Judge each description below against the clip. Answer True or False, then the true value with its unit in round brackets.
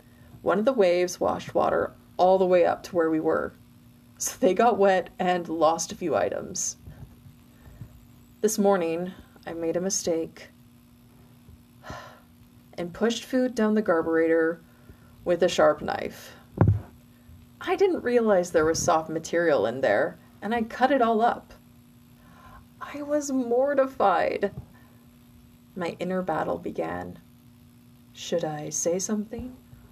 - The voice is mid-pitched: True (175 Hz)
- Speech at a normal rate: False (130 wpm)